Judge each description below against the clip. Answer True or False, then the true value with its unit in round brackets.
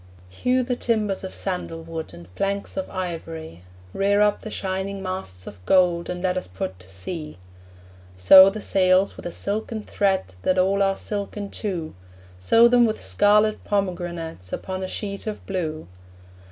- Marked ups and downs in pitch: False (3.8 semitones)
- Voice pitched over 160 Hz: True (185 Hz)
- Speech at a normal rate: True (165 wpm)